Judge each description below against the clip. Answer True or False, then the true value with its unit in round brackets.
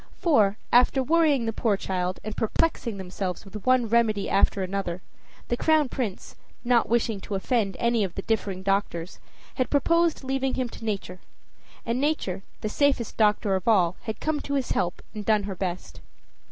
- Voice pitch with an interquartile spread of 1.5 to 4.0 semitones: False (4.7 semitones)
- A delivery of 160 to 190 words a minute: True (175 wpm)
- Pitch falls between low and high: False (220 Hz)